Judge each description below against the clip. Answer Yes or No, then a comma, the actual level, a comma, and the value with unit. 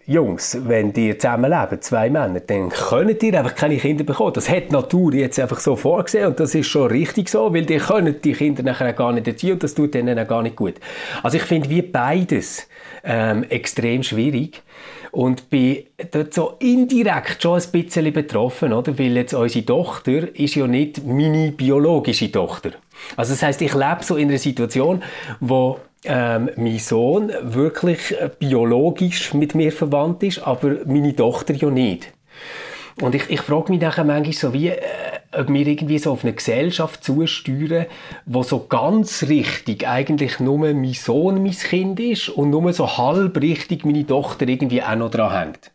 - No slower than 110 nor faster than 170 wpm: No, average, 180 wpm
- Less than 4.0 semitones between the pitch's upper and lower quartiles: No, average, 4.3 semitones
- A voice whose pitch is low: No, medium, 150 Hz